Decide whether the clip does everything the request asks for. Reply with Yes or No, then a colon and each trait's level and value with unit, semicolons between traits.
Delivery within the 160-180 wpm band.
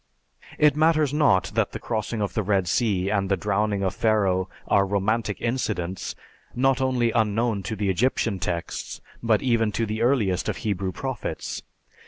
Yes: average, 165 wpm